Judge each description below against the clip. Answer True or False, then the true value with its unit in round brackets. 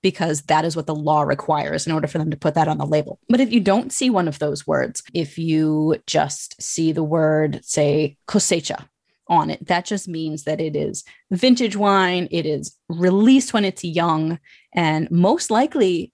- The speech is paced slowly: False (195 wpm)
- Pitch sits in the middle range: True (165 Hz)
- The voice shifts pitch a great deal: False (3.9 semitones)